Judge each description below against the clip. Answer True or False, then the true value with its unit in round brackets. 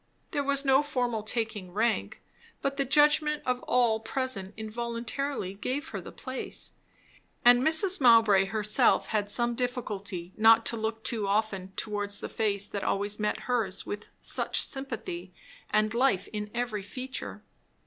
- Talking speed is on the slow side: False (150 wpm)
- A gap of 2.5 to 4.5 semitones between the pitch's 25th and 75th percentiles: True (3.7 semitones)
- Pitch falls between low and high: False (225 Hz)